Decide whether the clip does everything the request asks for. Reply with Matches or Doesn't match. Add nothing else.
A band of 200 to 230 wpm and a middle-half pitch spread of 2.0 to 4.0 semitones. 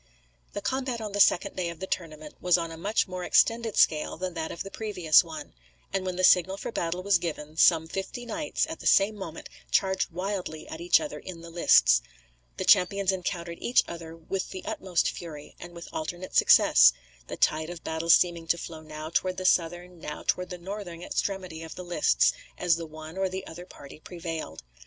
Matches